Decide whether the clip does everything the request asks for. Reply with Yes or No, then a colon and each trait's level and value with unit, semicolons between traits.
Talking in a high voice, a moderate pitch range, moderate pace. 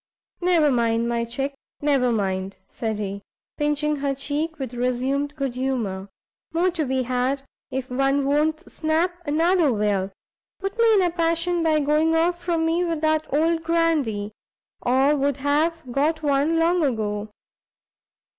Yes: very high, 285 Hz; average, 4.6 semitones; average, 150 wpm